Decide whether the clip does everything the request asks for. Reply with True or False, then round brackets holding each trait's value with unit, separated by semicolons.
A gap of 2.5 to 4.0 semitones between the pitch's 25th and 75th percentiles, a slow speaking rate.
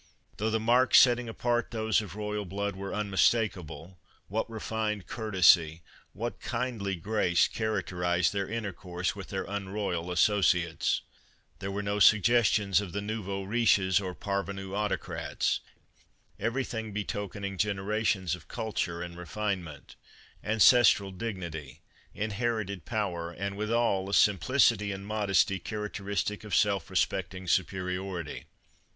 True (2.8 semitones; 125 wpm)